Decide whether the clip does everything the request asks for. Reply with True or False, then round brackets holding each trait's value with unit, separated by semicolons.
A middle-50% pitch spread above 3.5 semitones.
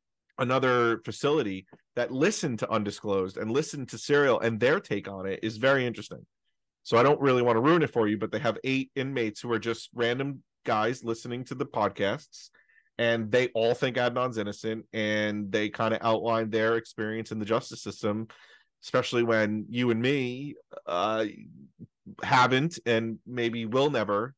False (2.7 semitones)